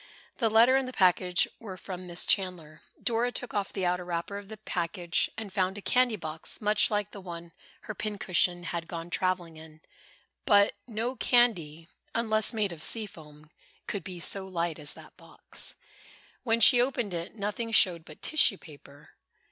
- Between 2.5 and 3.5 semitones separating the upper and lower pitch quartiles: No, average, 4.2 semitones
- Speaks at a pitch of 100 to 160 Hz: No, high, 190 Hz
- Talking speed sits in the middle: Yes, average, 175 wpm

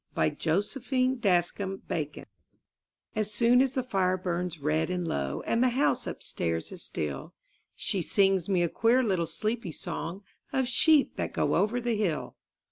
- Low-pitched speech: No, high, 195 Hz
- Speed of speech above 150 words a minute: Yes, average, 170 wpm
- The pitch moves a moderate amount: No, wide, 6.2 semitones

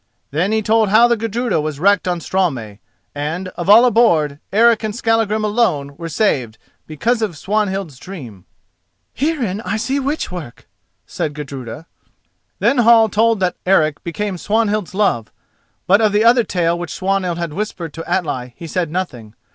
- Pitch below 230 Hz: Yes, high, 190 Hz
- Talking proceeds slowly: No, average, 165 wpm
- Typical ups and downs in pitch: No, wide, 5.9 semitones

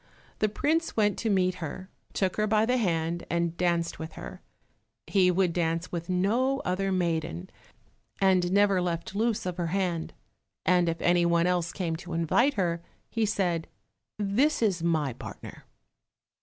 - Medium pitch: Yes, medium, 180 Hz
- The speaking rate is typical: Yes, average, 160 wpm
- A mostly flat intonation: No, average, 3.1 semitones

